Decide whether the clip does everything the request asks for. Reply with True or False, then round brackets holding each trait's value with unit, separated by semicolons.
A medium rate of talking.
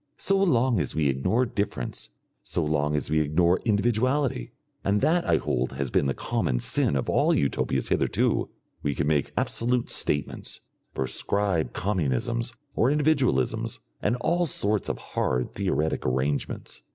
True (145 wpm)